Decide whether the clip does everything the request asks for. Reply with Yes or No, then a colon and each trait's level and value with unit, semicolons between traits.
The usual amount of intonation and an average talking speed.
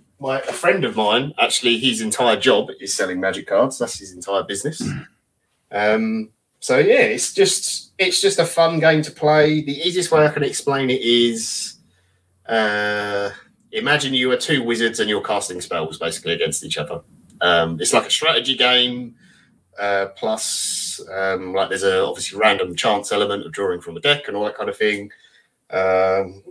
No: wide, 7.5 semitones; average, 180 wpm